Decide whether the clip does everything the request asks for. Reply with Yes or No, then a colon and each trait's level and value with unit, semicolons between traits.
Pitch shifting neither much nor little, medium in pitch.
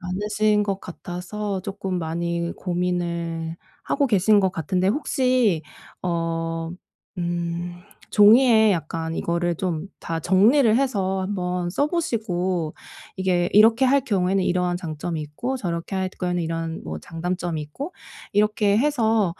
Yes: average, 3.7 semitones; medium, 180 Hz